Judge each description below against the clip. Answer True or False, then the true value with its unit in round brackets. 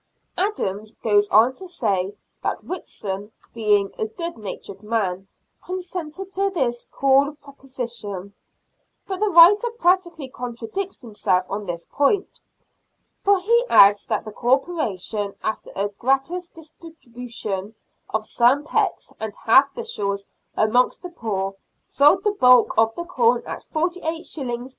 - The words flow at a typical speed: False (130 wpm)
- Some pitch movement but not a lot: False (8.6 semitones)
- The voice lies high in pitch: True (250 Hz)